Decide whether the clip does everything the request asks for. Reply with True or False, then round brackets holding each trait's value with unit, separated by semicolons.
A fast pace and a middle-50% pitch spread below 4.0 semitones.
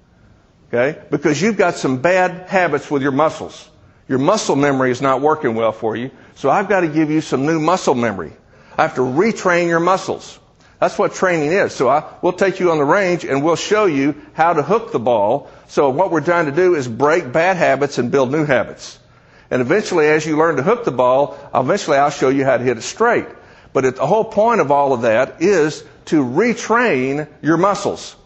False (215 wpm; 4.6 semitones)